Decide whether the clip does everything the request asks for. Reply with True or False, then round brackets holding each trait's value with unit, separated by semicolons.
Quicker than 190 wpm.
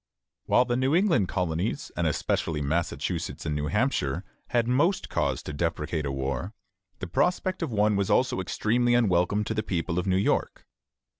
False (170 wpm)